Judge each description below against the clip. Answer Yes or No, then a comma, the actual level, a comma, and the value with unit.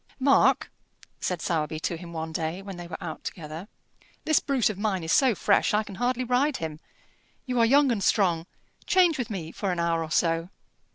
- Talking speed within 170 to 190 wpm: No, fast, 205 wpm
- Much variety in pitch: Yes, wide, 6.7 semitones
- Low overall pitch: No, medium, 185 Hz